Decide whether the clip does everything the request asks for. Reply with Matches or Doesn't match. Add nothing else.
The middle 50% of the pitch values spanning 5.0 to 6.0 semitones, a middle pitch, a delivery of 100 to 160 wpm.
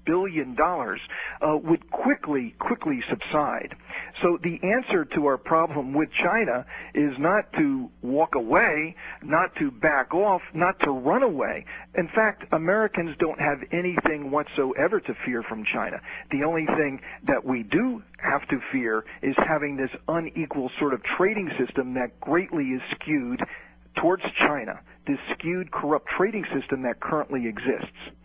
Matches